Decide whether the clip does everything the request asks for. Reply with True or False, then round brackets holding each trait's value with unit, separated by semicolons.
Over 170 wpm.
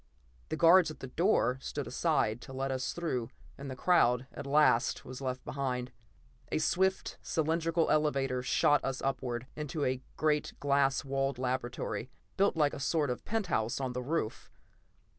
False (160 wpm)